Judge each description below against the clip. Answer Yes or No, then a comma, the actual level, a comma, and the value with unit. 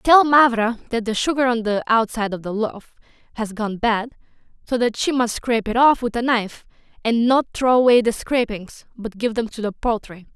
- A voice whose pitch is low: No, high, 230 Hz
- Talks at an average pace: No, fast, 210 wpm